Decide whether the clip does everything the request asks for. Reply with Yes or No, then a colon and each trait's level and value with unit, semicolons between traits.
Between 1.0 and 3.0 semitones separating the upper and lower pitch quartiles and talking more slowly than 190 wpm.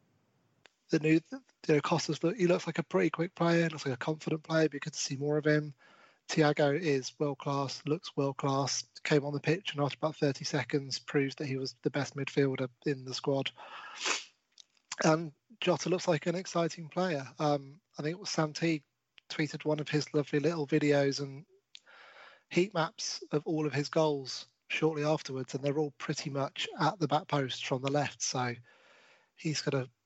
No: average, 2.7 semitones; average, 195 wpm